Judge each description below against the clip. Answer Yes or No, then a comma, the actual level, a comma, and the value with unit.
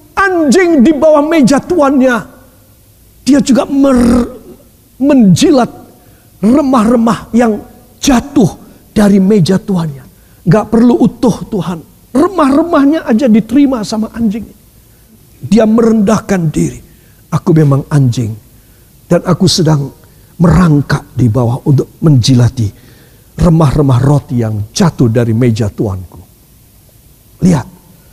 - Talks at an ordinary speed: Yes, average, 100 wpm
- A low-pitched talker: No, medium, 180 Hz